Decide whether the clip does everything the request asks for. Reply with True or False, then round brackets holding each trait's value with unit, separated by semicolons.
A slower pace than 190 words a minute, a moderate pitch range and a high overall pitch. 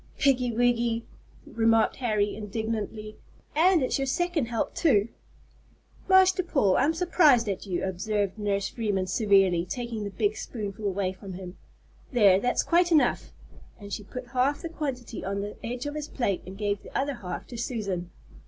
True (165 wpm; 4.9 semitones; 225 Hz)